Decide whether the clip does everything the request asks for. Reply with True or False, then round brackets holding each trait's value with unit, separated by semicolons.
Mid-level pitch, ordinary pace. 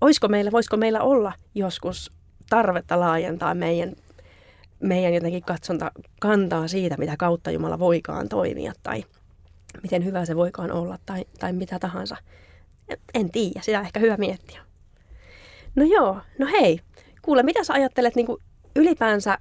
True (180 Hz; 140 wpm)